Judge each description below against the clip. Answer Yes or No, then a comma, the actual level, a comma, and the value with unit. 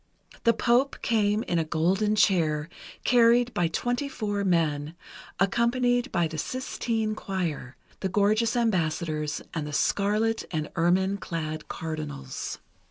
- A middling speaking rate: No, slow, 125 wpm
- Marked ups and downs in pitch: Yes, wide, 6.1 semitones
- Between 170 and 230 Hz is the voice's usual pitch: Yes, high, 190 Hz